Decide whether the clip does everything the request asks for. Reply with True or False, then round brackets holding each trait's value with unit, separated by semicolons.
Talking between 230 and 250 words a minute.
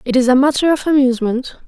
False (215 wpm)